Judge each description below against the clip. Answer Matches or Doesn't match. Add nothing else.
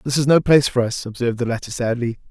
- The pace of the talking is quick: Matches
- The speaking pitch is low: Matches